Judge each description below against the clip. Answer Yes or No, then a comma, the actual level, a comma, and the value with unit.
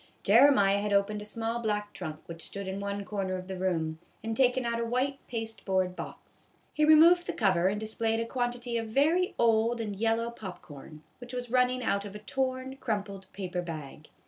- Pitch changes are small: No, average, 4.0 semitones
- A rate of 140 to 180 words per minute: No, average, 200 wpm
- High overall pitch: Yes, high, 220 Hz